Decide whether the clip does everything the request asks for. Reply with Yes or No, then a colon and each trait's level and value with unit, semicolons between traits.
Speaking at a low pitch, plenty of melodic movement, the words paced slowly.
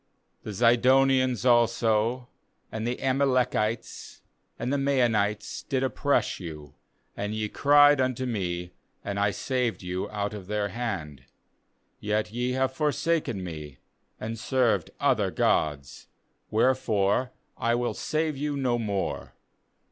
No: low, 115 Hz; average, 4.2 semitones; slow, 125 wpm